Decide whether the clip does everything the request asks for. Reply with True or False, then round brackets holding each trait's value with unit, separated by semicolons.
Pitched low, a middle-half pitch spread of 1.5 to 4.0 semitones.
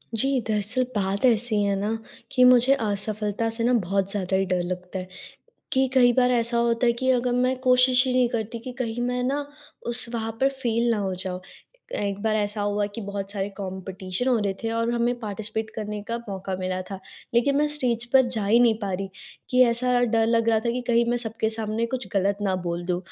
False (225 Hz; 3.5 semitones)